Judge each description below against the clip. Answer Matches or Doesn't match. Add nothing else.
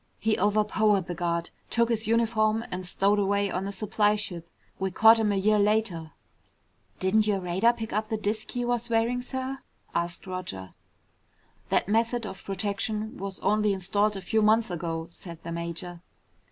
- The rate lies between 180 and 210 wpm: Doesn't match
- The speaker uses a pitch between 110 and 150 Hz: Doesn't match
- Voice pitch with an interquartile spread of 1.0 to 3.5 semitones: Matches